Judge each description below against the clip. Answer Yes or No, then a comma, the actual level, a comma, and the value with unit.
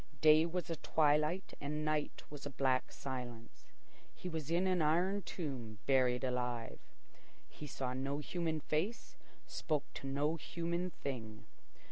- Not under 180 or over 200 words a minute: No, average, 140 wpm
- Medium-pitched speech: Yes, medium, 150 Hz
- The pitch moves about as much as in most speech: Yes, average, 4.0 semitones